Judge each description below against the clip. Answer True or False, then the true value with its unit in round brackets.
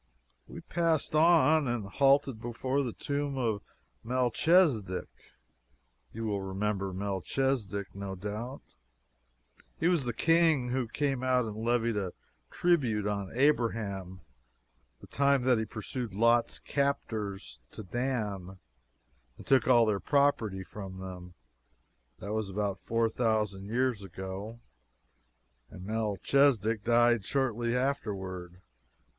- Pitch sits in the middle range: False (115 Hz)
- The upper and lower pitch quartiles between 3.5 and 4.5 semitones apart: False (4.9 semitones)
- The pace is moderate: False (115 wpm)